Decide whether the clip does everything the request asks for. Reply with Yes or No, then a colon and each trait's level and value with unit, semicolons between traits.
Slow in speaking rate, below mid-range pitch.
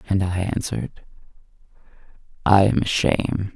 Yes: slow, 100 wpm; very low, 95 Hz